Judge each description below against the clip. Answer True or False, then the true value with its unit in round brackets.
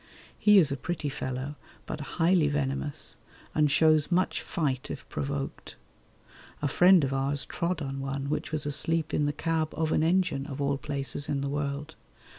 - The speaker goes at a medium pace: True (175 wpm)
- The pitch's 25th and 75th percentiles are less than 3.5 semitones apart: True (2.4 semitones)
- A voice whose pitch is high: False (145 Hz)